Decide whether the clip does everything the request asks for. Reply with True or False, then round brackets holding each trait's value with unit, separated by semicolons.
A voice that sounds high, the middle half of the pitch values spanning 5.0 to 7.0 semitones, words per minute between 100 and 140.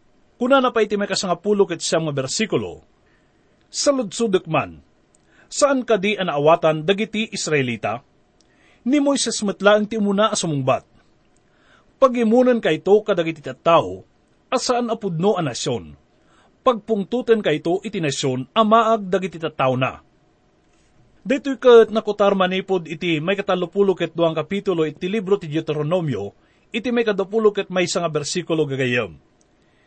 True (195 Hz; 5.6 semitones; 135 wpm)